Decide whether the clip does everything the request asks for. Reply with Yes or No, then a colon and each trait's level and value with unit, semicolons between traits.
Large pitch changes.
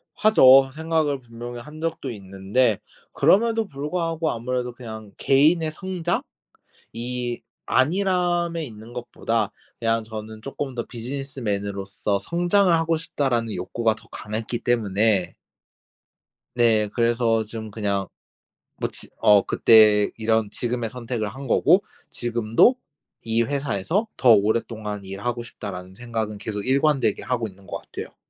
No: average, 4.8 semitones